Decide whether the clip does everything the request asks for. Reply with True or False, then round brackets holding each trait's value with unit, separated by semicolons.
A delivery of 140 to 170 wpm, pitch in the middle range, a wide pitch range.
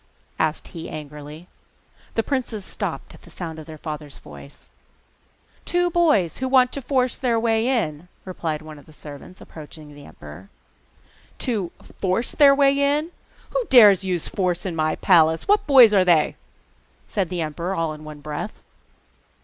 True (165 wpm; 180 Hz; 8.0 semitones)